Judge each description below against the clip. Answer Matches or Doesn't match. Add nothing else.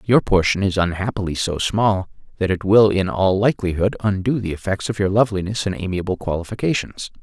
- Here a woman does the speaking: Doesn't match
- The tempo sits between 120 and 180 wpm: Matches